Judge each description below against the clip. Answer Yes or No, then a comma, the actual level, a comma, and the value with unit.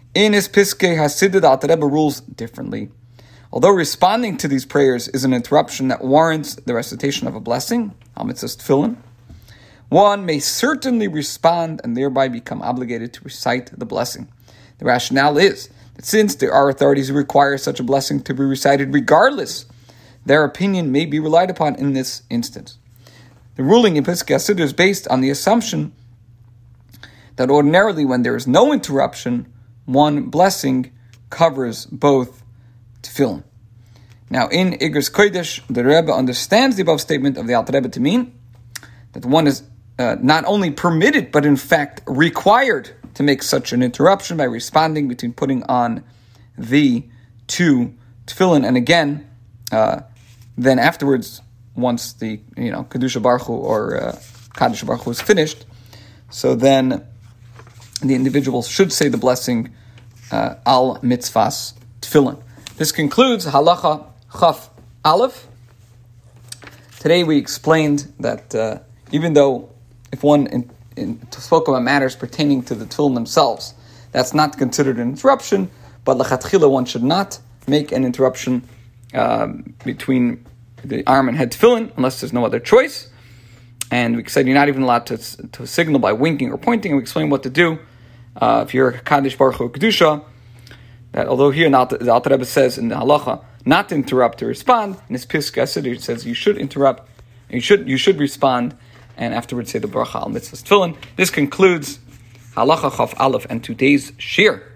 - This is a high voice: No, low, 130 Hz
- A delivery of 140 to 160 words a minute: Yes, average, 155 wpm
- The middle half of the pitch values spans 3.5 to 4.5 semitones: Yes, average, 3.8 semitones